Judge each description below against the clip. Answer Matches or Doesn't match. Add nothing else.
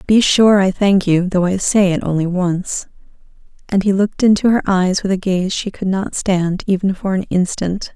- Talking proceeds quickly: Matches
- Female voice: Matches